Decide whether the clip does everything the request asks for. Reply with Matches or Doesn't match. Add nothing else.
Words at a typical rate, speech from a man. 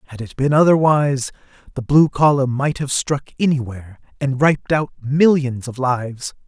Matches